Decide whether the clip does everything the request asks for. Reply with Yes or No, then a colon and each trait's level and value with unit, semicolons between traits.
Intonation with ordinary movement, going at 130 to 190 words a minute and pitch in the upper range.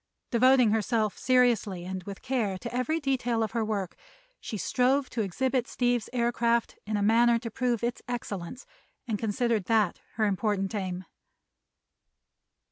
Yes: average, 3.1 semitones; average, 145 wpm; high, 230 Hz